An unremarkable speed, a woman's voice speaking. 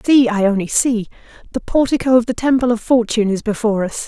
Yes: average, 175 wpm; female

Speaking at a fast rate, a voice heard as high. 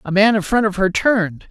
Yes: fast, 280 wpm; high, 200 Hz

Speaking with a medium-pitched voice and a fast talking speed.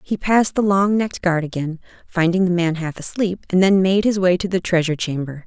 Yes: medium, 180 Hz; fast, 230 wpm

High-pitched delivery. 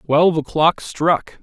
No: medium, 160 Hz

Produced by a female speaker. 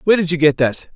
No: male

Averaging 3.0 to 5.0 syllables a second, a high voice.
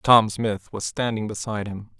No: 4.7 syllables/s; low, 105 Hz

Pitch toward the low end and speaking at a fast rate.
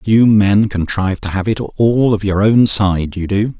Yes: low, 105 Hz; fast, 215 wpm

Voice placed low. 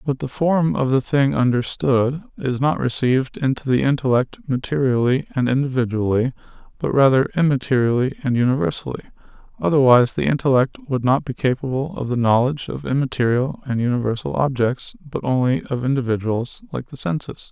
Yes: low, 130 Hz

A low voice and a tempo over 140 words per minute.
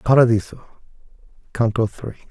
No: low, 115 Hz; slow, 80 wpm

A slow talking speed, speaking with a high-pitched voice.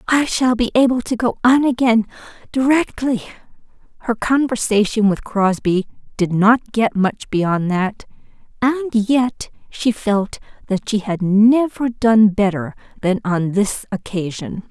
Yes: slow, 130 wpm; high, 220 Hz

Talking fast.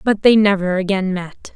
No: average, 195 wpm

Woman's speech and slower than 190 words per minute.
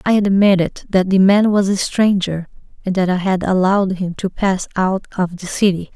No: female; average, 200 wpm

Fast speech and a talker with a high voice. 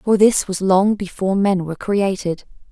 No: average, 175 wpm; high, 195 Hz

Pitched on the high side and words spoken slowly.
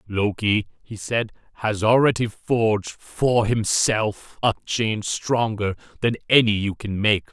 No: low, 110 Hz; slow, 130 wpm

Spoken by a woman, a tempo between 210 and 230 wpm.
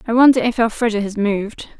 No: female; average, 200 wpm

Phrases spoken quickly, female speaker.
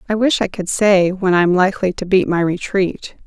Yes: fast, 240 wpm; female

